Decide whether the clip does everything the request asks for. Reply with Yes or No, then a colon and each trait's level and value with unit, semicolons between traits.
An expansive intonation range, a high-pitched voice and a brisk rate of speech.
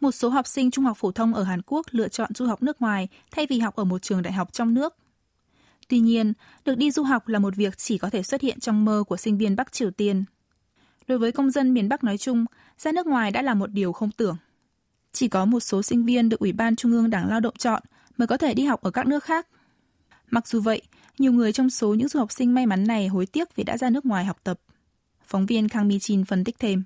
No: average, 3.7 semitones; high, 230 Hz; fast, 270 wpm